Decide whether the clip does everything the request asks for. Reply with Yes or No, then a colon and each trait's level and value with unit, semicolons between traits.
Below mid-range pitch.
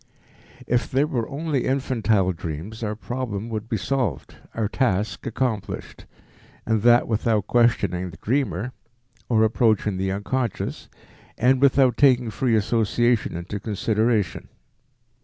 Yes: low, 115 Hz